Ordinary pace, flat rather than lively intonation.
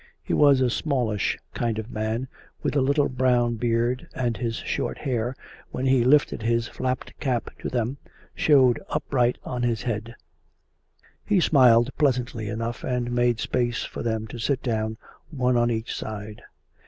Yes: average, 160 wpm; narrow, 2.1 semitones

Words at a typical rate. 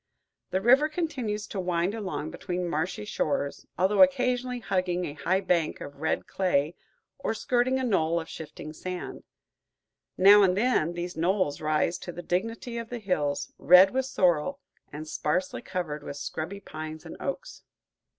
Yes: average, 155 wpm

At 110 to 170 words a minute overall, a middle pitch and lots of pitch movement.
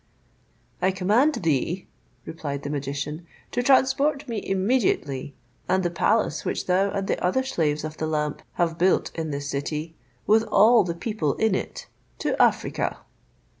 Yes: average, 155 wpm; medium, 180 Hz; wide, 6.2 semitones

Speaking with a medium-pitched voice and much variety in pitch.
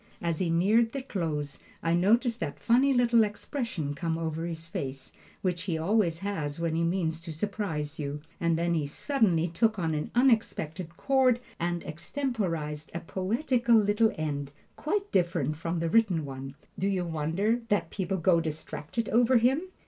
Yes: medium, 175 Hz; wide, 5.9 semitones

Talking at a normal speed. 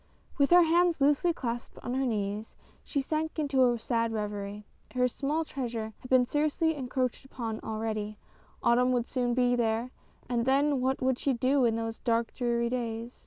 Yes: average, 175 wpm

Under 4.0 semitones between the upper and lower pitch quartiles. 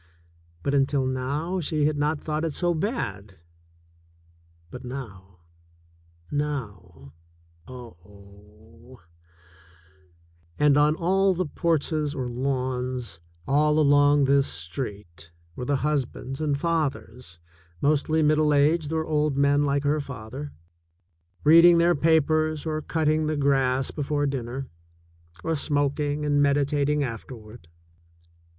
Yes: average, 3.6 semitones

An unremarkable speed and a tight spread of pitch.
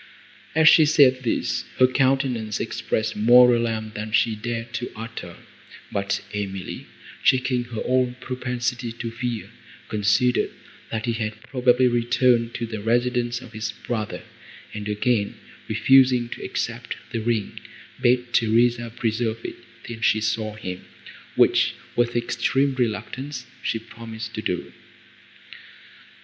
No: slow, 130 wpm; narrow, 2.1 semitones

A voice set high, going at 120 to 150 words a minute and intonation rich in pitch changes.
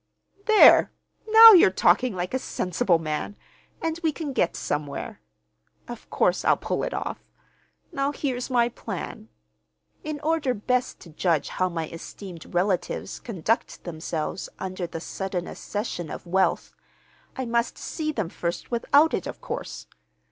Yes: high, 205 Hz; average, 145 wpm; wide, 7.6 semitones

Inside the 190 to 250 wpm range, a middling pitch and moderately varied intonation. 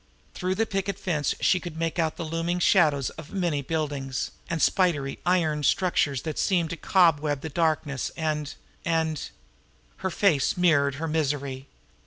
No: average, 155 wpm; medium, 160 Hz; average, 3.2 semitones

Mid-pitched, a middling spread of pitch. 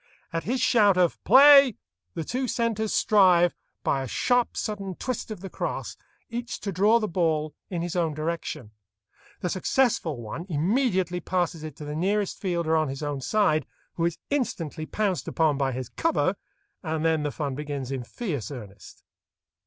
No: medium, 175 Hz; wide, 5.7 semitones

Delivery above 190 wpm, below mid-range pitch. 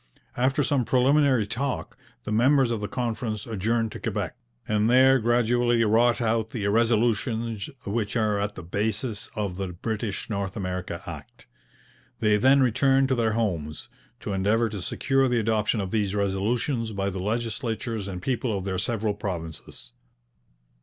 No: average, 155 wpm; low, 110 Hz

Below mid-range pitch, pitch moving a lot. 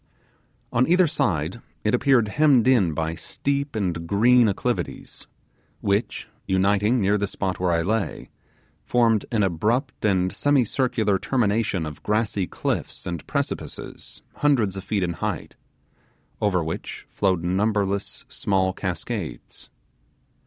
No: low, 105 Hz; average, 4.3 semitones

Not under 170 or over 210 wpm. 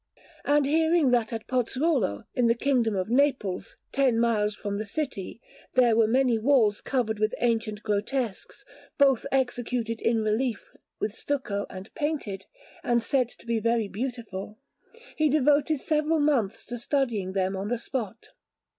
No: average, 150 wpm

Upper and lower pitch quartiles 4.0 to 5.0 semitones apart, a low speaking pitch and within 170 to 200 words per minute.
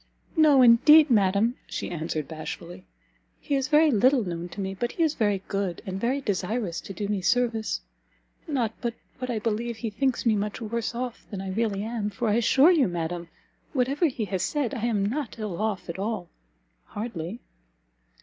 No: average, 4.3 semitones; high, 220 Hz; average, 190 wpm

